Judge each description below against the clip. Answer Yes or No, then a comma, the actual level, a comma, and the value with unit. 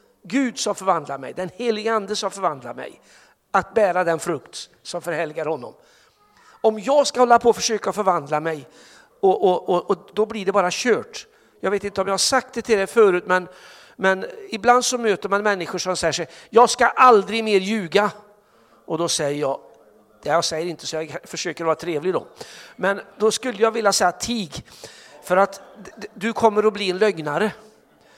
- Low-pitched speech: No, high, 200 Hz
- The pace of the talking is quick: No, average, 185 wpm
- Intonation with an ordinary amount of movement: Yes, average, 4.3 semitones